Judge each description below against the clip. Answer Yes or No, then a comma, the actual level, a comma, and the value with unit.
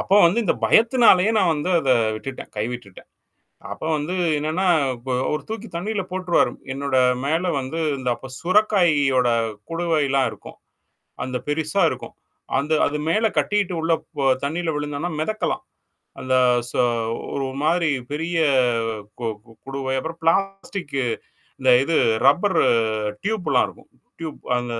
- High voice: No, medium, 160 Hz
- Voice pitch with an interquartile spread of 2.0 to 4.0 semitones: No, average, 5.2 semitones